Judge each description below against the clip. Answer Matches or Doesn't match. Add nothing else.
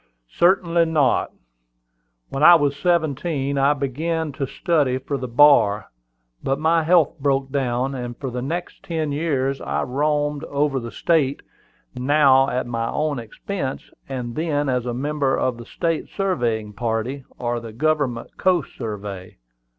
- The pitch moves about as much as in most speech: Matches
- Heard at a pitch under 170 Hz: Matches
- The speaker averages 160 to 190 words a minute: Doesn't match